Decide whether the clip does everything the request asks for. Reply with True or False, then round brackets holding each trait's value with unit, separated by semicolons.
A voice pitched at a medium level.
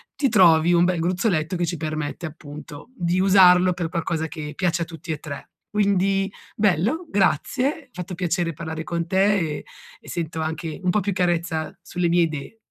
True (175 Hz)